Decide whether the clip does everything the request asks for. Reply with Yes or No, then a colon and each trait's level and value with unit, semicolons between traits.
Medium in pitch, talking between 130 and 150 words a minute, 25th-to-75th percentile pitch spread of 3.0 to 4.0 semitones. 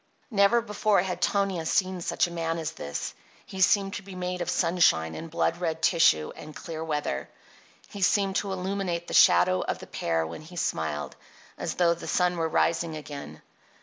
No: medium, 170 Hz; average, 185 wpm; average, 3.4 semitones